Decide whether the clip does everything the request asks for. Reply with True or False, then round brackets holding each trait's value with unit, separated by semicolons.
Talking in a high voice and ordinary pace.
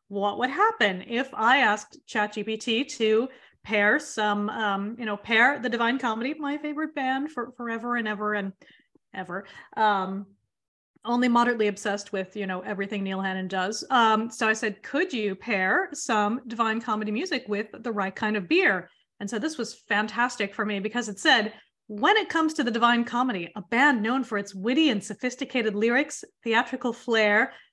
True (225 Hz; 180 wpm)